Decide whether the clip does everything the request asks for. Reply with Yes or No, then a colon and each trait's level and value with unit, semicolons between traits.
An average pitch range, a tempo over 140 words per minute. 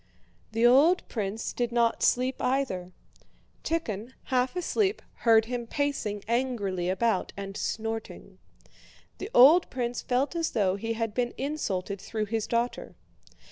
No: average, 3.7 semitones; slow, 135 wpm